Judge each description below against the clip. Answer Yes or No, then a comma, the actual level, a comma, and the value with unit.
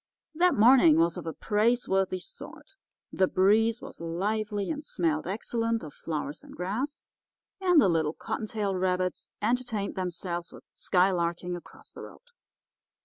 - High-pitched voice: Yes, high, 195 Hz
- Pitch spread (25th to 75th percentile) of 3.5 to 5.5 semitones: Yes, average, 4.8 semitones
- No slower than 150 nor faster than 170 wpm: No, average, 140 wpm